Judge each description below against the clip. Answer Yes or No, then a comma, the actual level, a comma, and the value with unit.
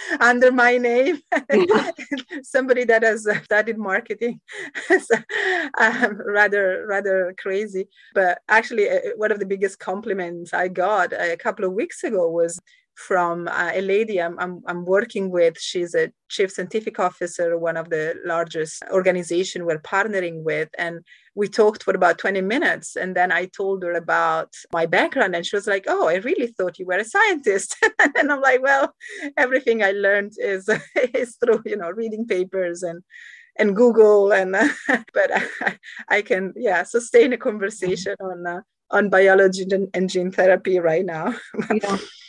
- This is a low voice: No, high, 200 Hz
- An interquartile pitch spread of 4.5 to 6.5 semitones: Yes, average, 5.0 semitones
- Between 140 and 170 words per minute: Yes, average, 165 wpm